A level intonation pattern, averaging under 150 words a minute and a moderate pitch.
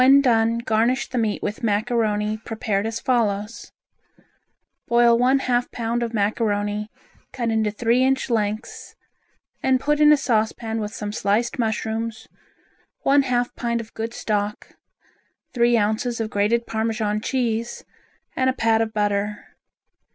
No: narrow, 2.2 semitones; average, 140 wpm; high, 225 Hz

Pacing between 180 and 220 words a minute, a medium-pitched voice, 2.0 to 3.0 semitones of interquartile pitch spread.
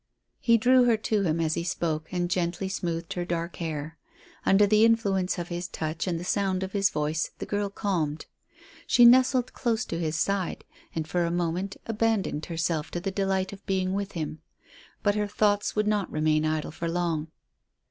No: average, 190 wpm; medium, 180 Hz; average, 3.7 semitones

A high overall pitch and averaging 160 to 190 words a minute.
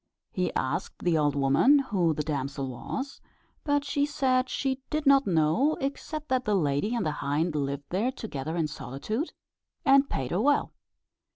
Yes: high, 200 Hz; average, 170 wpm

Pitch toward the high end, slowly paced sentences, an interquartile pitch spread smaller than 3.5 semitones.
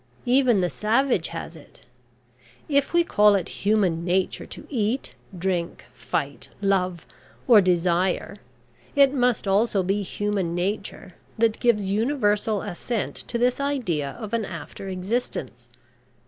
No: high, 205 Hz; slow, 130 wpm; average, 4.5 semitones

